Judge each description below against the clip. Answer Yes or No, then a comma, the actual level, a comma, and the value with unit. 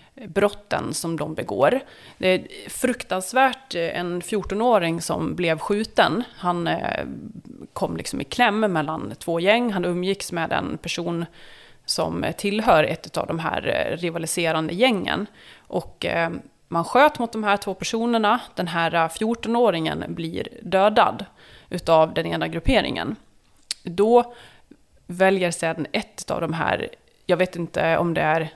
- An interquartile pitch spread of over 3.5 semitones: Yes, average, 4.5 semitones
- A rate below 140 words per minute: Yes, average, 130 wpm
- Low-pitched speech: No, medium, 180 Hz